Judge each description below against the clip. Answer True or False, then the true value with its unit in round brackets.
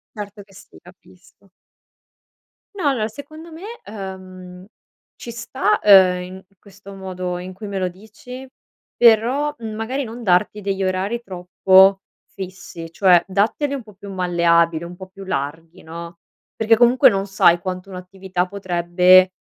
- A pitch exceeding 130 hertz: True (190 Hz)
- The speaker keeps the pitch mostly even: False (3.0 semitones)